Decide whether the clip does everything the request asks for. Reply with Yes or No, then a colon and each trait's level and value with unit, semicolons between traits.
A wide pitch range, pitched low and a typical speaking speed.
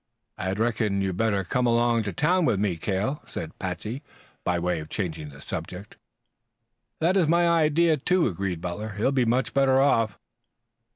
Yes: wide, 6.7 semitones; low, 110 Hz; average, 175 wpm